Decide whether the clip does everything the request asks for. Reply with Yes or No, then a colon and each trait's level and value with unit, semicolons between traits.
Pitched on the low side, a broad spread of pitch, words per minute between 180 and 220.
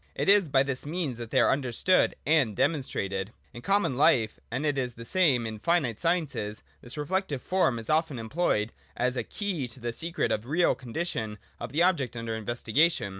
Yes: low, 130 Hz; wide, 6.2 semitones; average, 200 wpm